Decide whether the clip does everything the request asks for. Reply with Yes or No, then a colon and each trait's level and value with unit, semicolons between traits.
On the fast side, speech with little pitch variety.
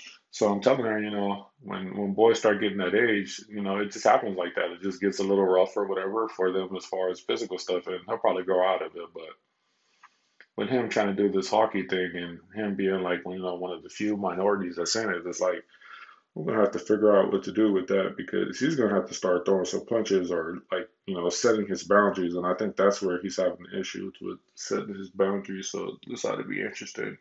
Yes: fast, 255 wpm; narrow, 1.8 semitones